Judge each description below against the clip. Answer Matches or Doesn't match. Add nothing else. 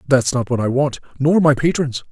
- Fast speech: Matches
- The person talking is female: Doesn't match